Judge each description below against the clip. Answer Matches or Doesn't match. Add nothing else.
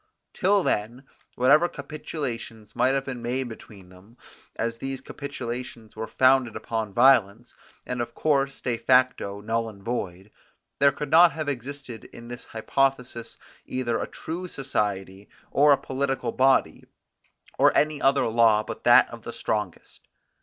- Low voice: Matches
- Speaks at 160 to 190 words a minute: Doesn't match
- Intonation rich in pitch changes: Doesn't match